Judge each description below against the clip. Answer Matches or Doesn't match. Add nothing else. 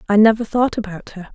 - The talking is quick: Matches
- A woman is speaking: Matches